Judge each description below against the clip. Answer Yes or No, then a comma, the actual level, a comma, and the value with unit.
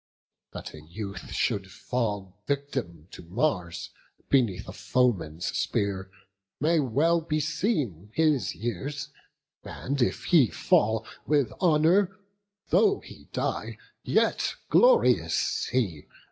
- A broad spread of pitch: Yes, wide, 7.8 semitones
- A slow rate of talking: Yes, slow, 105 wpm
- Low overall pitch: Yes, low, 125 Hz